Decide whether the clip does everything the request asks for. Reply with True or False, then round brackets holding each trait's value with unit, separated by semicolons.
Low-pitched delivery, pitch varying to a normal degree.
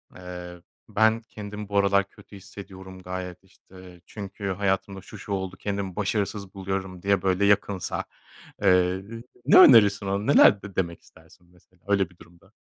False (95 Hz; 1.7 semitones)